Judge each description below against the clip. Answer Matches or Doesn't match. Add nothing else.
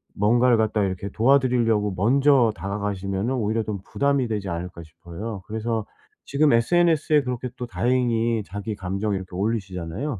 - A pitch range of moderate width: Matches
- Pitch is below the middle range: Matches